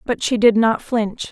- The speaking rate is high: Yes, fast, 230 wpm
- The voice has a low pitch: No, high, 225 Hz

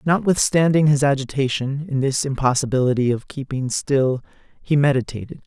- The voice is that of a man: Yes, male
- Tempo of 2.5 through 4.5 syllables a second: No, 5.3 syllables/s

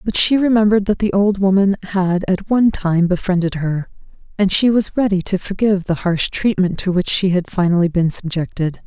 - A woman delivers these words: Yes, female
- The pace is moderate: Yes, average, 195 wpm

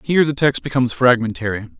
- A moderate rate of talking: Yes, average, 165 wpm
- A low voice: Yes, low, 130 Hz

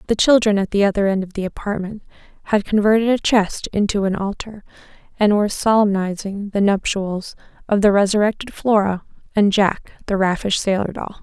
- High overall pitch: Yes, high, 205 Hz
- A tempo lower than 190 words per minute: Yes, average, 165 wpm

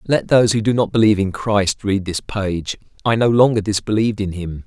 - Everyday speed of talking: No, fast, 220 wpm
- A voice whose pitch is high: No, low, 105 Hz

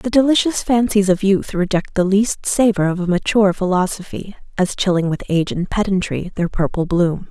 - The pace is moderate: Yes, average, 180 wpm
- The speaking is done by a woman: Yes, female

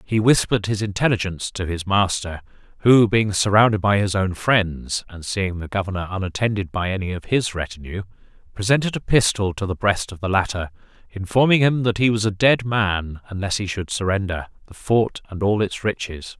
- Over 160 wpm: Yes, average, 185 wpm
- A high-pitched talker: No, low, 100 Hz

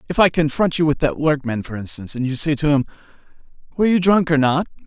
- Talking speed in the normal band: No, fast, 235 wpm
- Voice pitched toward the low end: No, medium, 150 Hz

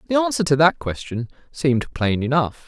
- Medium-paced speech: Yes, average, 180 wpm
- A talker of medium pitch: Yes, medium, 150 Hz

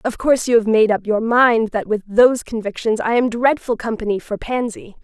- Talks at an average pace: Yes, average, 190 wpm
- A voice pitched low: No, high, 230 Hz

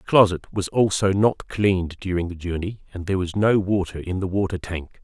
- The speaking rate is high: Yes, fast, 215 wpm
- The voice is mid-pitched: No, very low, 95 Hz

